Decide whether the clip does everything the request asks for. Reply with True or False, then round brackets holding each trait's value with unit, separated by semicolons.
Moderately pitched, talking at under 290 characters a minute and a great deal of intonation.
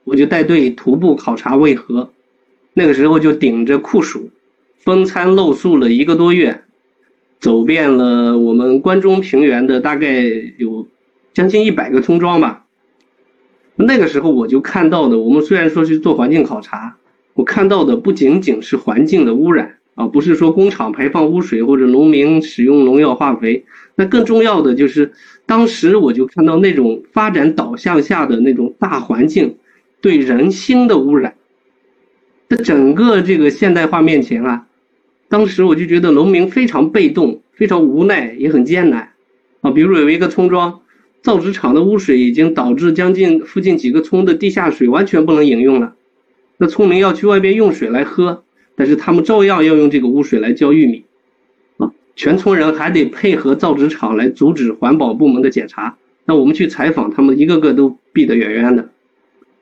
True (160 Hz; 270 characters per minute; 6.5 semitones)